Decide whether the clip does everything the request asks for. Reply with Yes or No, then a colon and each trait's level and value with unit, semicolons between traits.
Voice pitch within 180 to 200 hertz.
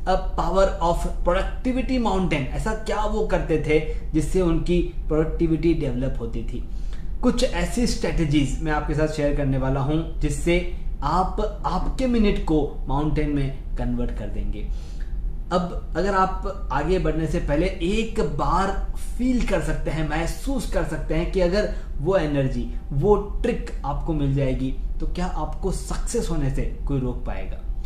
No: medium, 160 Hz